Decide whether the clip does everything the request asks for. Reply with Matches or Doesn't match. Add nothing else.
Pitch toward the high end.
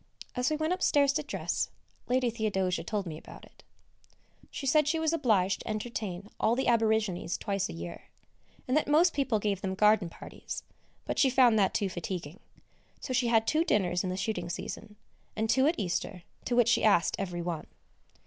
Matches